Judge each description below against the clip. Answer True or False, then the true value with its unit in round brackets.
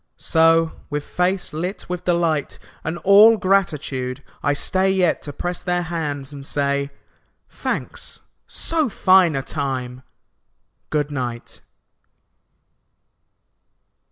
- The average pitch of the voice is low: False (160 Hz)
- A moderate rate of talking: False (105 wpm)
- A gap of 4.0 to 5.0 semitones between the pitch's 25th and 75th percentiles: True (4.3 semitones)